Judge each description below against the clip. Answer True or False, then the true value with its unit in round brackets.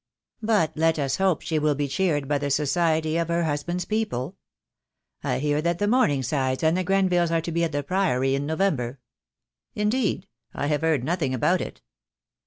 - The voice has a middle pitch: True (160 Hz)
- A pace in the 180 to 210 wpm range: True (185 wpm)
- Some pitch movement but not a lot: True (4.0 semitones)